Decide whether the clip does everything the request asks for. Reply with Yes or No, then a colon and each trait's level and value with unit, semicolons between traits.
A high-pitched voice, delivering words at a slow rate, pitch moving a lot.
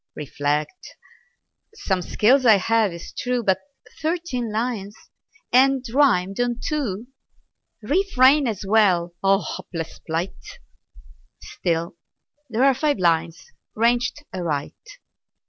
Yes: high, 220 Hz; slow, 105 wpm; wide, 6.2 semitones